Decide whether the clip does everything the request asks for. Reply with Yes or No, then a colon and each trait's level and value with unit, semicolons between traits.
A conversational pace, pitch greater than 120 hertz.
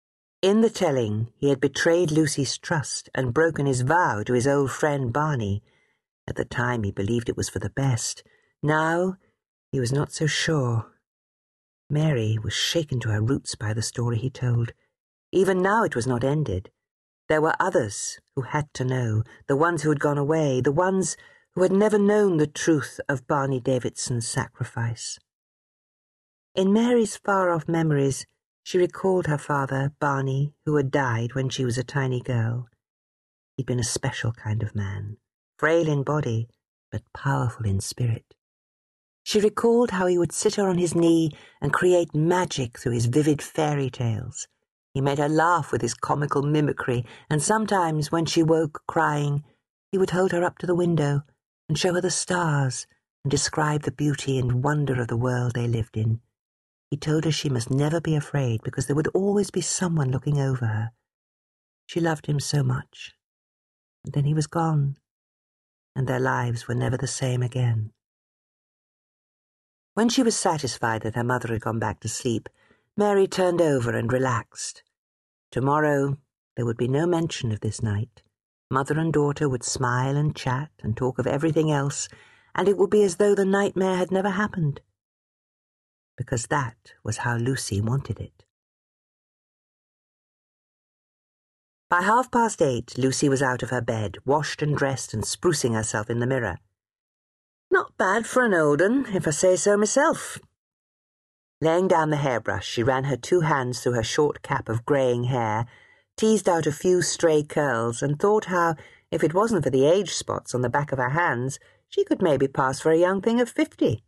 Yes: average, 175 wpm; medium, 140 Hz